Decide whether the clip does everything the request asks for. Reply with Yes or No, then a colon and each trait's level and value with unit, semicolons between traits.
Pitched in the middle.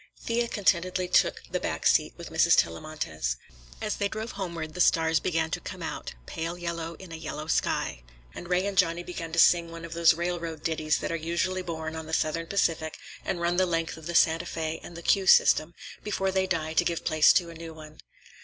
Yes: medium, 165 Hz